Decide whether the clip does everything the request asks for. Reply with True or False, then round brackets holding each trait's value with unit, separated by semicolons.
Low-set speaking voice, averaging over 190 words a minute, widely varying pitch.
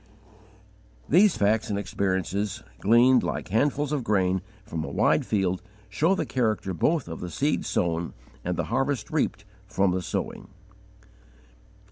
False (105 Hz; 140 wpm; 6.2 semitones)